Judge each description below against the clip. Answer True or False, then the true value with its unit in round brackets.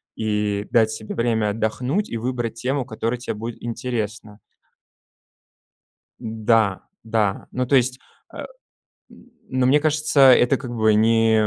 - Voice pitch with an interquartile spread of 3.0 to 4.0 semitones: False (2.5 semitones)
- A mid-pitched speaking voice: False (115 Hz)